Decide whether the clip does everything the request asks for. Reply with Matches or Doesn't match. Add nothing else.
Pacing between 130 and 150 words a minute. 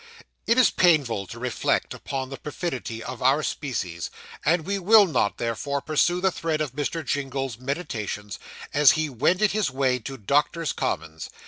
Doesn't match